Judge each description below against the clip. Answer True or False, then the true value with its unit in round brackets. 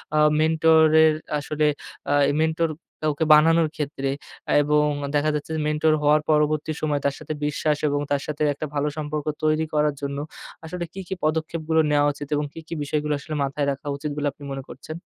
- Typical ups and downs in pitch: False (1.3 semitones)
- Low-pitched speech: False (150 Hz)